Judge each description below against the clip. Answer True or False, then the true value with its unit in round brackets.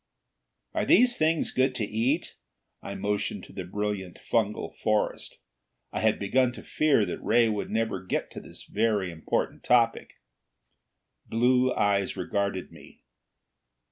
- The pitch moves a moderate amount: True (3.8 semitones)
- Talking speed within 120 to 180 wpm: True (140 wpm)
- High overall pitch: False (110 Hz)